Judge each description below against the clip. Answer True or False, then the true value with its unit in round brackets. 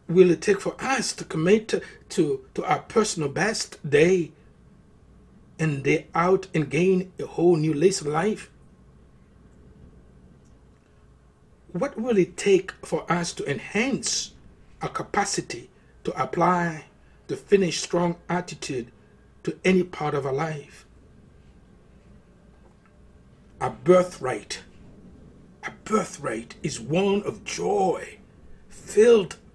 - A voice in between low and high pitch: True (175 Hz)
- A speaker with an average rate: False (110 wpm)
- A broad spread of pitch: False (4.7 semitones)